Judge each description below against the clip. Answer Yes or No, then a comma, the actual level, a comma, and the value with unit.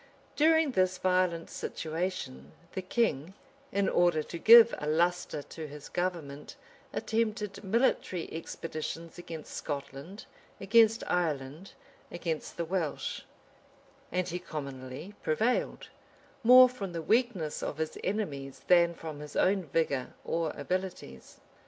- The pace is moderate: No, slow, 120 wpm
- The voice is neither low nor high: Yes, medium, 175 Hz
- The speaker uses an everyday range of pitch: Yes, average, 4.3 semitones